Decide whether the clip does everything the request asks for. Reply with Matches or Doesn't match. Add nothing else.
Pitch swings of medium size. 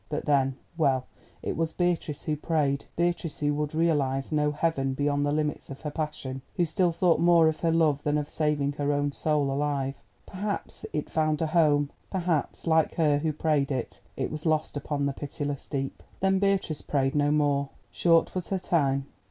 Doesn't match